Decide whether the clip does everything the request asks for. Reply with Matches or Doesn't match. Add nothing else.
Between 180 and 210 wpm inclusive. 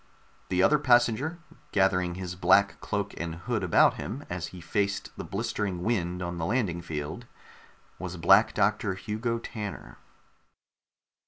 Doesn't match